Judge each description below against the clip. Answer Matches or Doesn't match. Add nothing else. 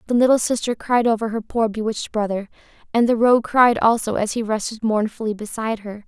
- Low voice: Doesn't match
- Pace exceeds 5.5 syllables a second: Matches